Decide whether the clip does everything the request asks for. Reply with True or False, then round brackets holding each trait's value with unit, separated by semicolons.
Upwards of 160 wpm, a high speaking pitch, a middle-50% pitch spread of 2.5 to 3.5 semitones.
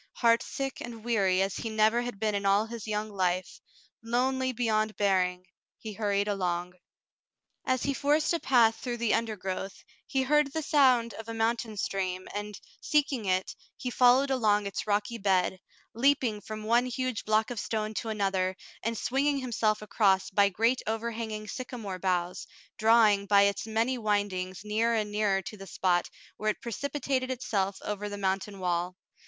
True (170 wpm; 215 Hz; 3.2 semitones)